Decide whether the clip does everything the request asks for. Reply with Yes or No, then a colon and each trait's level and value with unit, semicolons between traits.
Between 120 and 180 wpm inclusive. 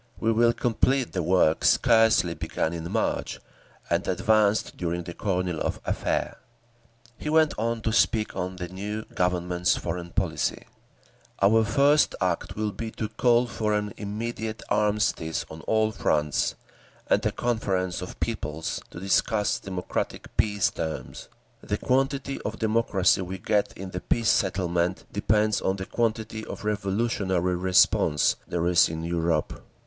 Yes: average, 145 wpm